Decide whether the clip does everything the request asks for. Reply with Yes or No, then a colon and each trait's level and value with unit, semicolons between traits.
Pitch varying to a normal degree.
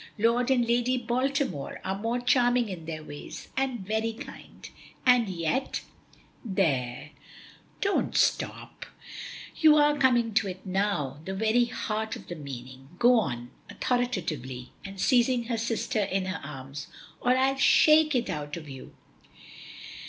No: wide, 7.8 semitones